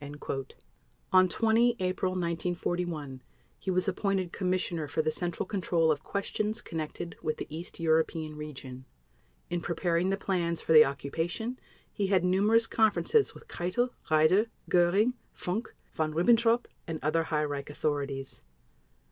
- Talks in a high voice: No, medium, 175 Hz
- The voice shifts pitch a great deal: No, average, 3.8 semitones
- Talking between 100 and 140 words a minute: Yes, slow, 135 wpm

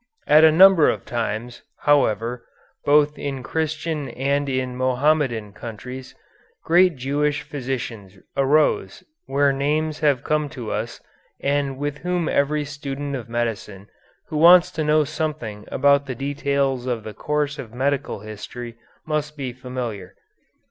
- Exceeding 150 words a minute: No, slow, 135 wpm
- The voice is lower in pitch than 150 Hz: Yes, medium, 140 Hz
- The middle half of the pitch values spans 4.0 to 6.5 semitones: No, average, 3.5 semitones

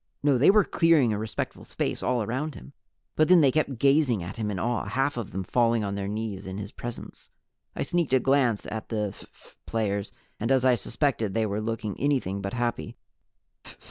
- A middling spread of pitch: Yes, average, 4.5 semitones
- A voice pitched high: No, low, 115 Hz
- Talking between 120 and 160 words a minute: No, fast, 205 wpm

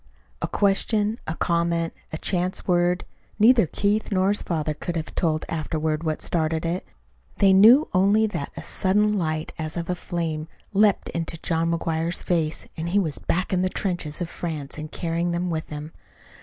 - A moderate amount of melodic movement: Yes, average, 3.1 semitones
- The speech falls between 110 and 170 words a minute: No, average, 180 wpm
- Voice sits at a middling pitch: Yes, medium, 170 Hz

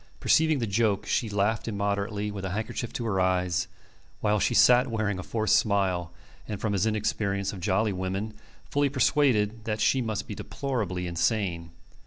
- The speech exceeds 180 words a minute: No, average, 170 wpm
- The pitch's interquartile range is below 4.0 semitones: Yes, average, 2.7 semitones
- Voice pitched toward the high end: No, low, 105 Hz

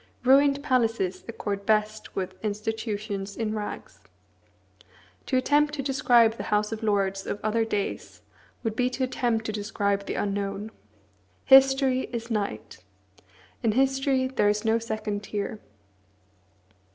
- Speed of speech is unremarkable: No, slow, 130 wpm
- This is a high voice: Yes, high, 220 Hz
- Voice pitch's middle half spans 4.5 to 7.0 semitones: No, average, 3.7 semitones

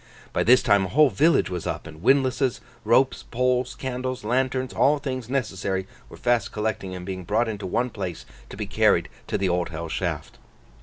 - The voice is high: No, low, 120 Hz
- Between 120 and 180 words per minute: No, average, 190 wpm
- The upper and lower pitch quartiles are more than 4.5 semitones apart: Yes, wide, 5.4 semitones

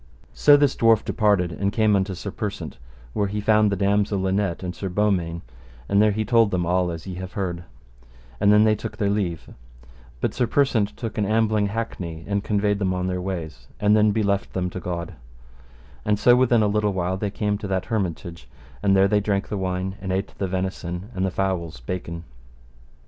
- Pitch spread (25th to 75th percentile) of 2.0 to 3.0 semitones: Yes, narrow, 2.4 semitones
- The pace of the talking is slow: No, fast, 205 wpm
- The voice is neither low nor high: No, low, 100 Hz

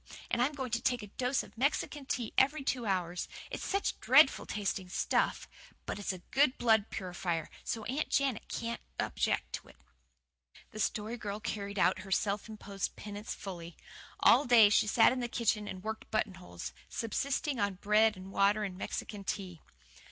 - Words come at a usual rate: Yes, average, 175 wpm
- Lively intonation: No, average, 3.7 semitones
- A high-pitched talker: Yes, high, 215 Hz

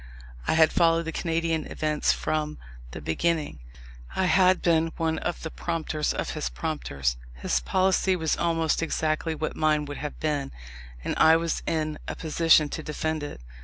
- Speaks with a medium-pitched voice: Yes, medium, 160 Hz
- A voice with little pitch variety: Yes, narrow, 1.5 semitones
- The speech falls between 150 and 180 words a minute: Yes, average, 165 wpm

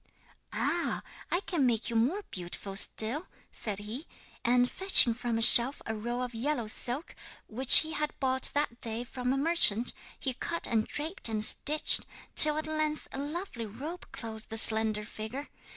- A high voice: Yes, high, 245 Hz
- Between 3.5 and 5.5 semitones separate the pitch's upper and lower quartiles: Yes, average, 5.2 semitones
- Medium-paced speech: Yes, average, 170 wpm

